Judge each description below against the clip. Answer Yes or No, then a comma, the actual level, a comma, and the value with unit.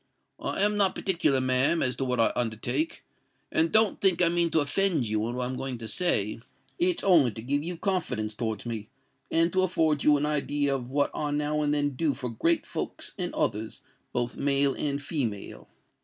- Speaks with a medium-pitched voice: Yes, medium, 145 Hz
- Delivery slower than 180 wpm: No, average, 200 wpm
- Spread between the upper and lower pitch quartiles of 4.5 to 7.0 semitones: Yes, wide, 5.4 semitones